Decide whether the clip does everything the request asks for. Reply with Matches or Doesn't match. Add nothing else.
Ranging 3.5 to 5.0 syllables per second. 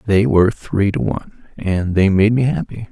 Matches